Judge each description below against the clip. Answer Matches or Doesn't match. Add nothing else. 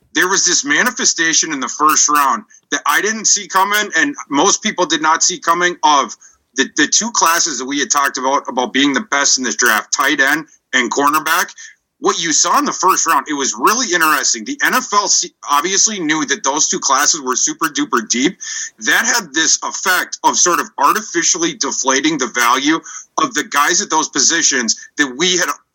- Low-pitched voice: Doesn't match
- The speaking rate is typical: Matches